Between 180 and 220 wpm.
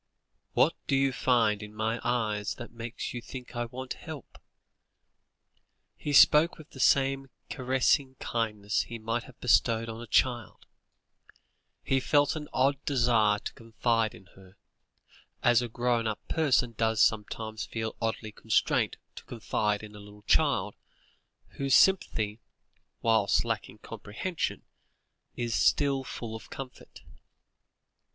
No: slow, 135 wpm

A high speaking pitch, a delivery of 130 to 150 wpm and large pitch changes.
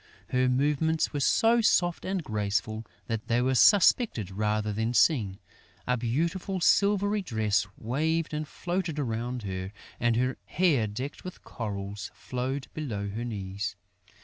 No: low, 125 Hz; average, 140 wpm; wide, 7.0 semitones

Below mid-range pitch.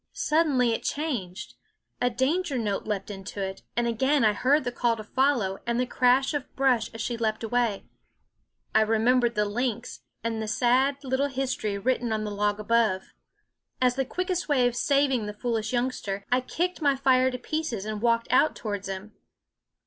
No: high, 240 Hz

